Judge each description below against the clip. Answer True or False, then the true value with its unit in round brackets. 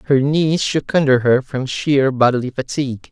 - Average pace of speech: True (175 wpm)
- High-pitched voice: False (135 Hz)